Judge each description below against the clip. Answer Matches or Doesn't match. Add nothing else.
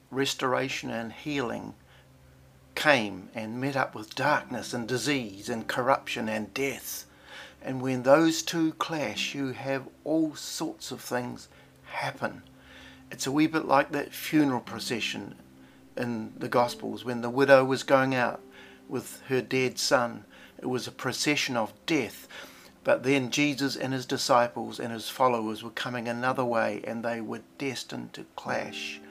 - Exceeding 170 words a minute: Doesn't match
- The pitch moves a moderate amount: Matches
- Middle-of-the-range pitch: Doesn't match